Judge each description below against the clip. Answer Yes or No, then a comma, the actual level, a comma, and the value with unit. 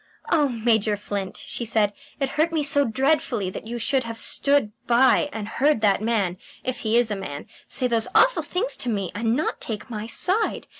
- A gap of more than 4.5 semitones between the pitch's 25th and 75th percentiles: Yes, average, 4.9 semitones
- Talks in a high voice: Yes, high, 235 Hz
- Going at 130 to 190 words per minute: No, average, 200 wpm